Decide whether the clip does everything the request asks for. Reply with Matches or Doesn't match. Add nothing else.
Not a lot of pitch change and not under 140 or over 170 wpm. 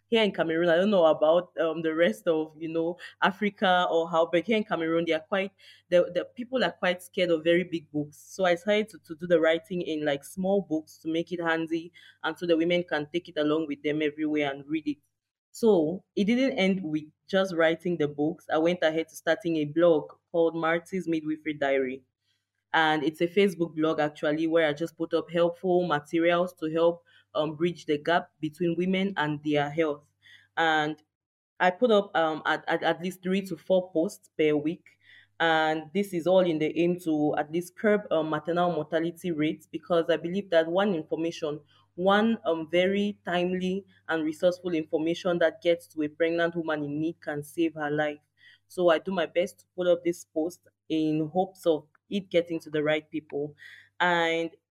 Doesn't match